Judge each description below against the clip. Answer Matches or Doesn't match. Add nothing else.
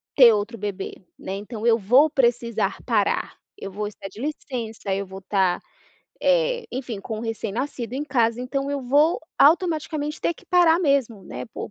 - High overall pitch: Matches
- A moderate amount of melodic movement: Doesn't match